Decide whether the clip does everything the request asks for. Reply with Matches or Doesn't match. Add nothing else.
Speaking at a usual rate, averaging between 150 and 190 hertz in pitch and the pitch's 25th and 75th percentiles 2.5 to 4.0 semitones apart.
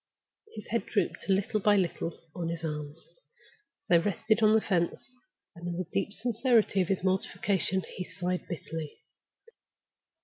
Matches